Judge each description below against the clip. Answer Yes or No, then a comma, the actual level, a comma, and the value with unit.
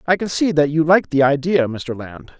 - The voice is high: No, medium, 150 Hz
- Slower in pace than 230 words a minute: No, fast, 250 wpm